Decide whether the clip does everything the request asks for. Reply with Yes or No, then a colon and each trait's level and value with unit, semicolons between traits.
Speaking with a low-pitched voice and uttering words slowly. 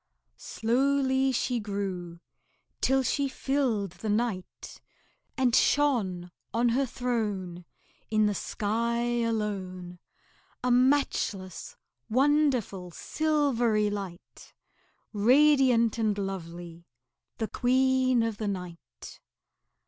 No: high, 225 Hz; slow, 90 wpm